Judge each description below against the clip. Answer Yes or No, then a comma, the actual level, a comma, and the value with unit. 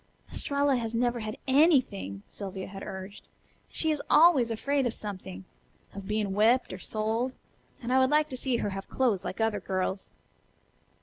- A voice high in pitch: Yes, high, 225 Hz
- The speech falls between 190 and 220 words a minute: No, average, 175 wpm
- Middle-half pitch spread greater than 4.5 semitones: Yes, average, 5.0 semitones